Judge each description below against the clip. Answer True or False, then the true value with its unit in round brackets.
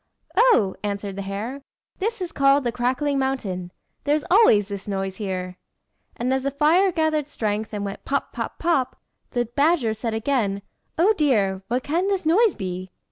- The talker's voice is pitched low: False (250 Hz)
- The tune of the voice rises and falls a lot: True (7.1 semitones)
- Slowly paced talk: False (170 wpm)